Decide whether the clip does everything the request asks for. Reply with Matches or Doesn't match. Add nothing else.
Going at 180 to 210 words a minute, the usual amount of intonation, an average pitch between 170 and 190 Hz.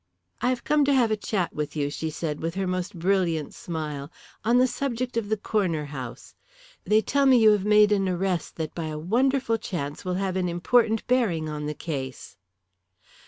Doesn't match